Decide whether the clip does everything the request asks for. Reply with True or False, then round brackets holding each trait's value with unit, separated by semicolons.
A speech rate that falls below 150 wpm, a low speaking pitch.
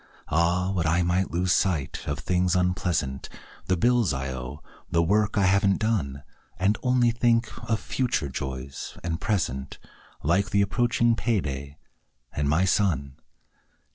True (140 wpm; 90 Hz)